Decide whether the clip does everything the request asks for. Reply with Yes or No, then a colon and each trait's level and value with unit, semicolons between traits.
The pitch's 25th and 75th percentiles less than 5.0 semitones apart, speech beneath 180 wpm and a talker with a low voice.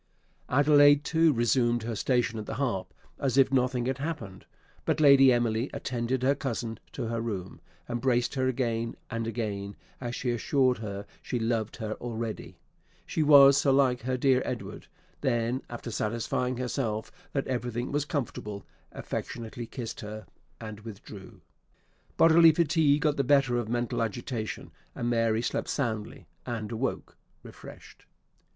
Yes: average, 3.0 semitones; average, 145 wpm; low, 120 Hz